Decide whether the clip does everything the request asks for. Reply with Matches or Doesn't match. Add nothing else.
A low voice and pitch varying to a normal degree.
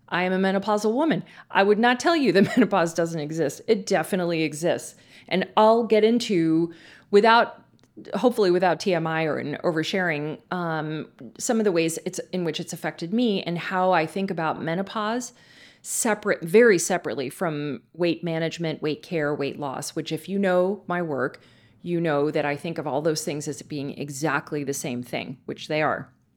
Doesn't match